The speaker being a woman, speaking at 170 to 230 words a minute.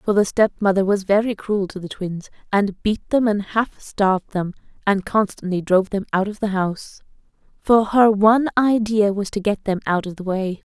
Yes: female; fast, 205 wpm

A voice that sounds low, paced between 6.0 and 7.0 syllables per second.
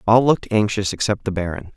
Yes: low, 105 Hz; 6.2 syllables/s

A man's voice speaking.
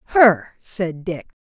No: female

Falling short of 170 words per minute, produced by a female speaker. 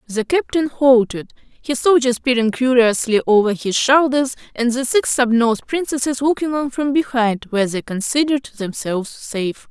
Yes: average, 150 wpm; female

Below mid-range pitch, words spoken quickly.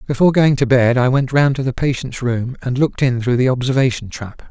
Yes: low, 130 Hz; fast, 240 wpm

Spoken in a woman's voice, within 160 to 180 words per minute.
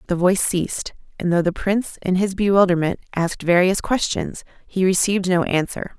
Yes: female; average, 170 wpm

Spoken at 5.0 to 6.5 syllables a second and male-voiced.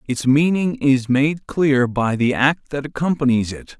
No: 4.1 syllables/s; male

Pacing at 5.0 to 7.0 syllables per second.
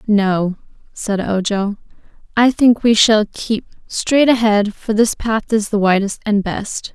No: 3.8 syllables/s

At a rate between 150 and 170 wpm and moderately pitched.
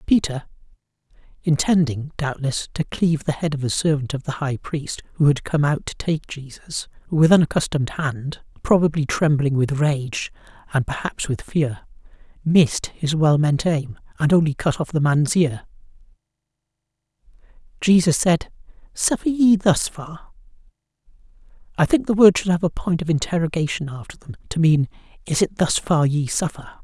Yes: average, 155 wpm; medium, 155 Hz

